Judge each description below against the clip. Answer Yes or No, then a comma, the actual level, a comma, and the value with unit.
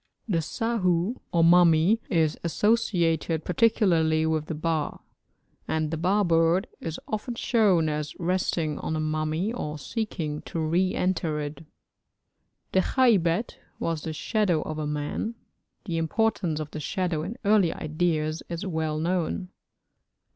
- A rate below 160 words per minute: Yes, average, 140 wpm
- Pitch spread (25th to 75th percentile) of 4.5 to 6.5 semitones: No, average, 3.2 semitones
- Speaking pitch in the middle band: Yes, medium, 165 Hz